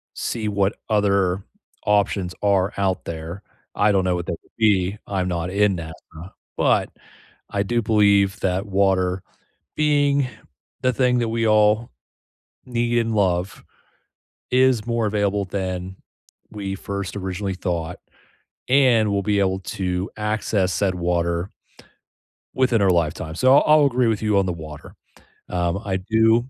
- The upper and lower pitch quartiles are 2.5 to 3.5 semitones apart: Yes, average, 3.2 semitones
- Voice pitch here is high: No, low, 100 Hz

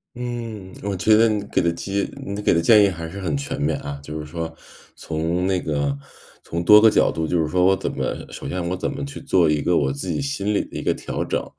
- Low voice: Yes, very low, 90 Hz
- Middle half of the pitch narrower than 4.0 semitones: No, average, 4.3 semitones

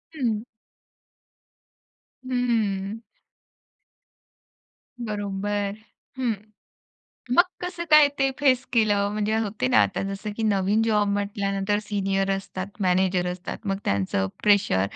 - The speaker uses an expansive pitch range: No, narrow, 2.5 semitones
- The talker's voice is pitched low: No, high, 205 Hz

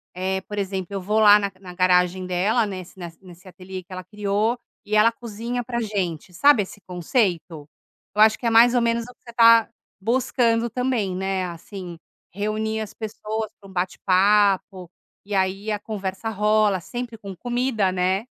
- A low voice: No, high, 205 Hz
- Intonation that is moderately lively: Yes, average, 3.3 semitones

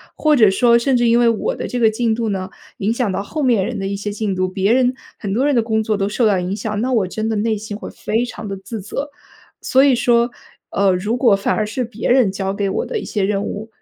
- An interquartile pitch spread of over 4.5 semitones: No, average, 3.3 semitones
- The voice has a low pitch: No, high, 220 Hz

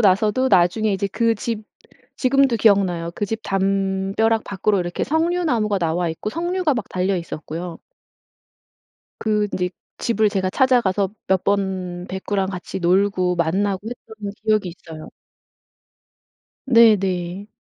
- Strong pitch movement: No, average, 3.3 semitones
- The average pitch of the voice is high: Yes, high, 200 Hz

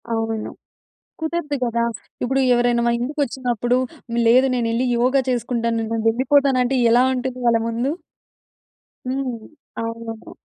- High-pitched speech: Yes, high, 245 Hz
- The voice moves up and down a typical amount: No, narrow, 2.2 semitones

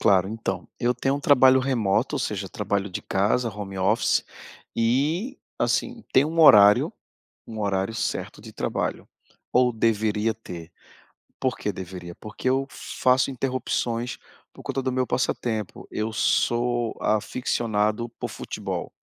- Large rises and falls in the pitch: No, average, 3.9 semitones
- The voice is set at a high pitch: No, low, 115 Hz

